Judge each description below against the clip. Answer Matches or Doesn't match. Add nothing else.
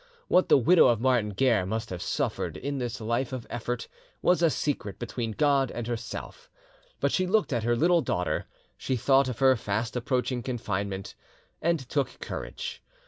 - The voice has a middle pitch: Doesn't match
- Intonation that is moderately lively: Matches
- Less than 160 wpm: Doesn't match